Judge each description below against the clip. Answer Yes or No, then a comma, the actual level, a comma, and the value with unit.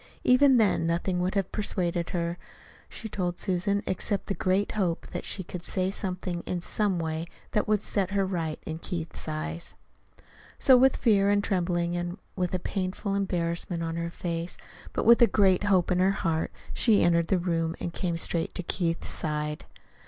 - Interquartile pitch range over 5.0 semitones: No, average, 2.8 semitones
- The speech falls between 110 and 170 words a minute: No, average, 180 wpm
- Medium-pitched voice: Yes, medium, 180 Hz